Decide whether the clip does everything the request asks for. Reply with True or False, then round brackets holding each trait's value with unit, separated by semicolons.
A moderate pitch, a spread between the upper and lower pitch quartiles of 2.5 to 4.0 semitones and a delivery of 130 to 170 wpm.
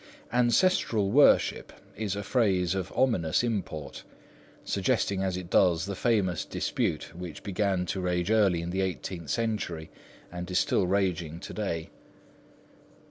False (95 Hz; 3.1 semitones; 135 wpm)